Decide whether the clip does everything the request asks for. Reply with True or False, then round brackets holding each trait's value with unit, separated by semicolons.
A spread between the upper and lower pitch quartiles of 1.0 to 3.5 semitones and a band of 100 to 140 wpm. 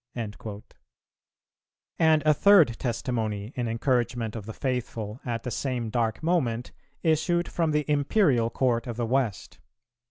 False (4.7 semitones; 135 wpm)